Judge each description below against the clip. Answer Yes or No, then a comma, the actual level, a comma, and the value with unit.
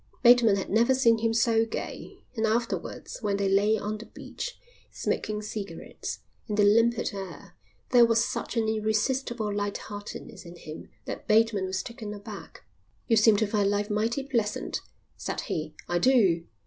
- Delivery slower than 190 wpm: Yes, average, 165 wpm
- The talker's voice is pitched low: No, high, 215 Hz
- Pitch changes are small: Yes, narrow, 2.1 semitones